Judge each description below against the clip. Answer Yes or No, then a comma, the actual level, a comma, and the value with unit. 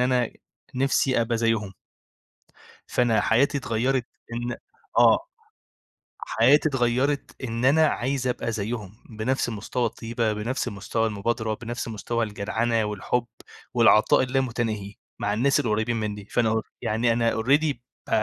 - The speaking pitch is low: Yes, low, 115 Hz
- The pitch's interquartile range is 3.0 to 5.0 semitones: No, narrow, 2.5 semitones